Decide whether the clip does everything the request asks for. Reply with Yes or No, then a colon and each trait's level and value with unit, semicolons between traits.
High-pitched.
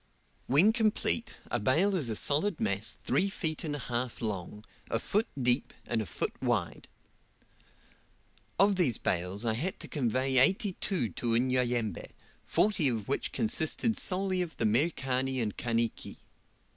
No: low, 130 Hz